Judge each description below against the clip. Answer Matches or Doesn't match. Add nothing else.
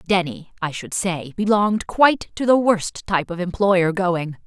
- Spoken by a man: Doesn't match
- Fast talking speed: Doesn't match